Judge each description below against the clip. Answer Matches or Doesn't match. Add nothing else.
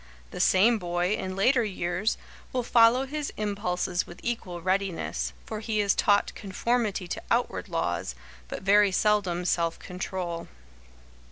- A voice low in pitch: Doesn't match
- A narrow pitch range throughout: Doesn't match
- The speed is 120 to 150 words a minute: Matches